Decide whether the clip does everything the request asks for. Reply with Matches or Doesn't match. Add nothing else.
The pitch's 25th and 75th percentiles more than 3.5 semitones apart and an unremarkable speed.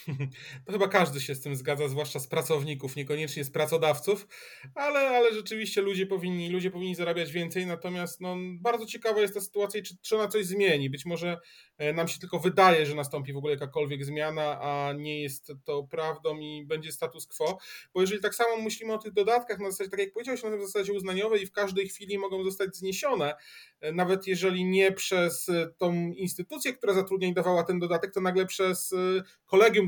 Doesn't match